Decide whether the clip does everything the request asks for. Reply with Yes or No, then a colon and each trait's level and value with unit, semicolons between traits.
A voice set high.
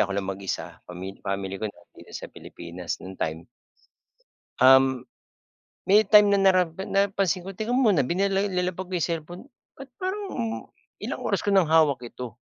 No: medium, 175 Hz